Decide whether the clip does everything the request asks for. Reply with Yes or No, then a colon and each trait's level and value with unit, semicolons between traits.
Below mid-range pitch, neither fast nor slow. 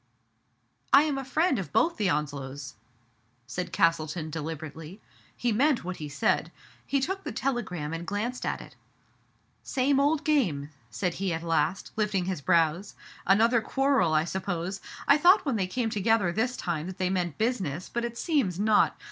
No: high, 190 Hz; average, 180 wpm